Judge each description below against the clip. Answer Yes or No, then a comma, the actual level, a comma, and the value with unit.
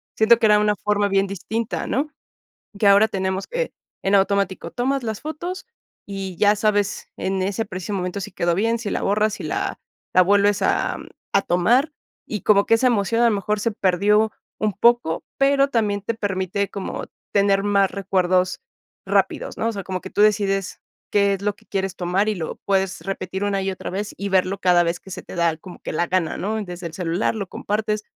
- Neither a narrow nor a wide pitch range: No, narrow, 2.2 semitones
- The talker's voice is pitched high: Yes, high, 200 Hz